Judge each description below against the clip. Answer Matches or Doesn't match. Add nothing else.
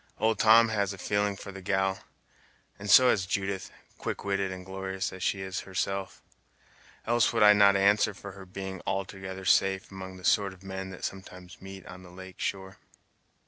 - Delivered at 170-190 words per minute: Matches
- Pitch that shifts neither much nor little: Doesn't match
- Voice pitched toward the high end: Doesn't match